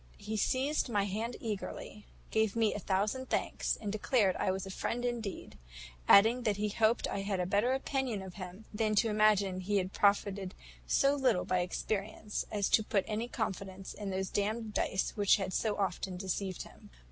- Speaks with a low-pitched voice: No, high, 205 Hz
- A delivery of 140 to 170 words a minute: No, average, 185 wpm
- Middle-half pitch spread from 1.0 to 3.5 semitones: Yes, narrow, 2.4 semitones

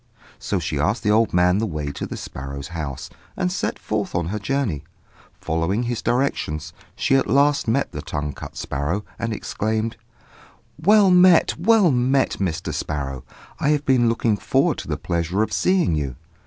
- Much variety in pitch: Yes, wide, 9.0 semitones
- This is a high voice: No, low, 105 Hz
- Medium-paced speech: Yes, average, 175 wpm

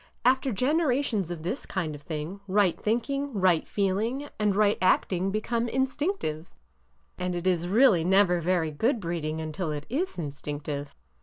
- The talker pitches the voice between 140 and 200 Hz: Yes, high, 190 Hz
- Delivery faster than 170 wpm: No, average, 155 wpm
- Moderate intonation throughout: No, wide, 6.5 semitones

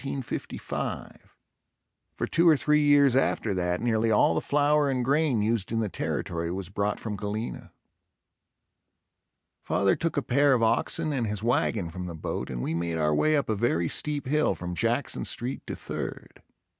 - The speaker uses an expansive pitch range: Yes, wide, 7.2 semitones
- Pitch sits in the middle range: No, low, 115 Hz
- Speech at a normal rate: Yes, average, 170 wpm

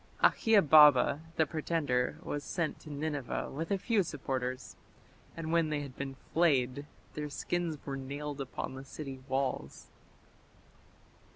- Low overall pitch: No, medium, 145 Hz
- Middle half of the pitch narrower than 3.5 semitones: Yes, average, 2.9 semitones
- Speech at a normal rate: No, slow, 130 wpm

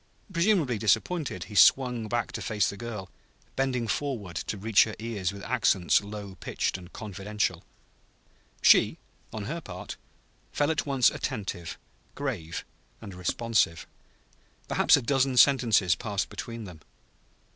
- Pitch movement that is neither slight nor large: Yes, average, 4.7 semitones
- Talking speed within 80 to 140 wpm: Yes, slow, 135 wpm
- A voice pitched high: No, low, 110 Hz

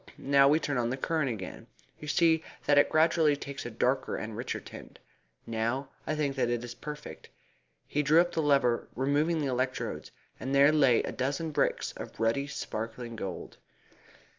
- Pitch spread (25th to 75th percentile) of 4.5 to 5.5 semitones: No, average, 3.6 semitones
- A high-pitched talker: No, medium, 140 Hz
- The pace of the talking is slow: No, average, 180 wpm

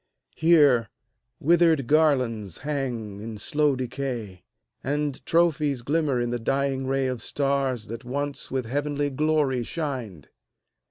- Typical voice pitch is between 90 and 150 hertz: Yes, low, 135 Hz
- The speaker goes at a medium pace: No, slow, 120 wpm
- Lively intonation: No, average, 3.4 semitones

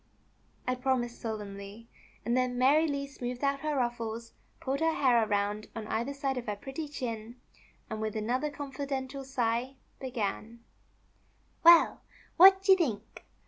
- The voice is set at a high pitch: Yes, very high, 250 Hz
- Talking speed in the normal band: Yes, average, 145 wpm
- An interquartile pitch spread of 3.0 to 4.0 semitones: Yes, average, 3.7 semitones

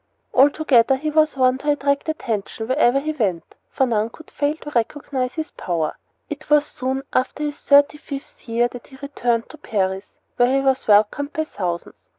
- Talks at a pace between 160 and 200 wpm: Yes, average, 180 wpm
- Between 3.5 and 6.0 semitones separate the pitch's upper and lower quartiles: Yes, average, 4.2 semitones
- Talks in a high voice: Yes, very high, 265 Hz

